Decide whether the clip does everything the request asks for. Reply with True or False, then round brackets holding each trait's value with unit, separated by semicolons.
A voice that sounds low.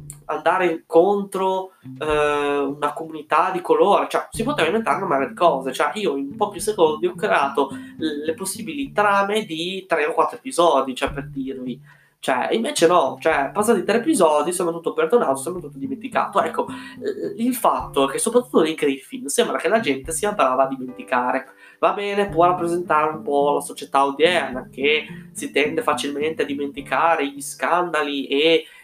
False (165 Hz)